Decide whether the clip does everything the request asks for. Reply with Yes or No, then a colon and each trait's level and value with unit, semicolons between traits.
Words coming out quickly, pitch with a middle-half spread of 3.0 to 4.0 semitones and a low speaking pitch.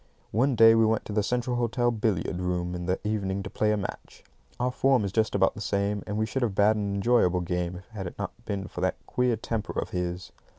Yes: fast, 245 wpm; average, 3.4 semitones; low, 105 Hz